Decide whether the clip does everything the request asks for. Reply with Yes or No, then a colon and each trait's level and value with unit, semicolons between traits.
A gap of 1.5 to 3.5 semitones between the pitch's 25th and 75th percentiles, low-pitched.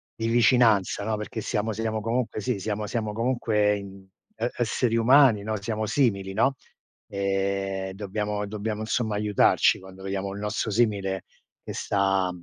Yes: narrow, 2.4 semitones; low, 105 Hz